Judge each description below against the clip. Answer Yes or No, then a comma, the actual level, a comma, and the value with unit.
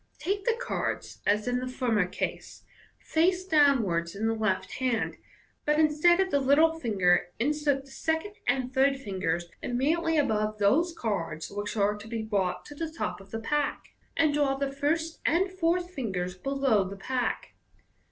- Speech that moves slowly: No, average, 170 wpm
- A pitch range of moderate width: No, wide, 7.1 semitones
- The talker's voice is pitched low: No, very high, 265 Hz